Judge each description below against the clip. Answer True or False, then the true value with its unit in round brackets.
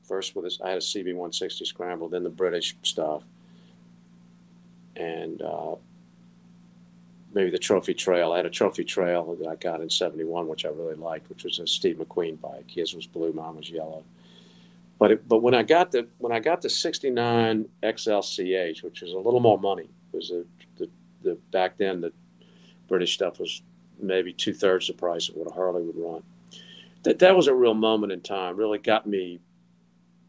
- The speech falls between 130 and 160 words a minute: False (190 wpm)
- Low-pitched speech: False (160 Hz)